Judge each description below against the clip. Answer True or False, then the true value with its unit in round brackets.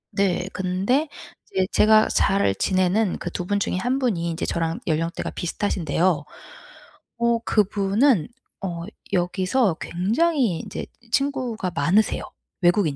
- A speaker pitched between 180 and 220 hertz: True (190 Hz)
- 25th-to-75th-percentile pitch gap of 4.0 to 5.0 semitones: True (4.3 semitones)